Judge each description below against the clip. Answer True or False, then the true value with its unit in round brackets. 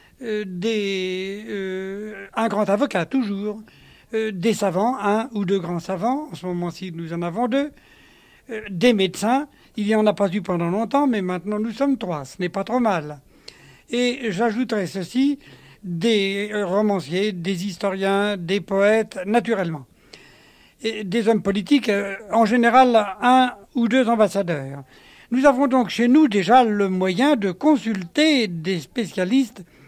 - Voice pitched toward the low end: False (210 Hz)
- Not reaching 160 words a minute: True (150 wpm)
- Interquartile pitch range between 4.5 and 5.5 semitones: False (3.7 semitones)